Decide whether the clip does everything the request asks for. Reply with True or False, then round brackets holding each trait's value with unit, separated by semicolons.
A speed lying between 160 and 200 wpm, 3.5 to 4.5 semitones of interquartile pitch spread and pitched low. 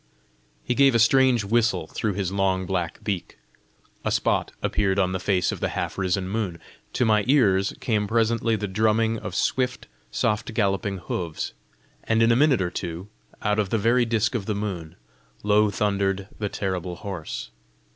False (175 wpm; 3.0 semitones; 105 Hz)